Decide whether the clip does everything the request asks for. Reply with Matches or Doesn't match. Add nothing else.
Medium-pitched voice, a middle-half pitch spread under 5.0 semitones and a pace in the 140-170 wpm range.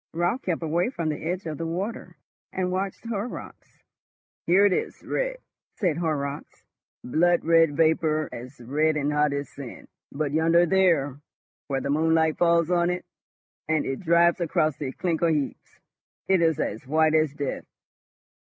Matches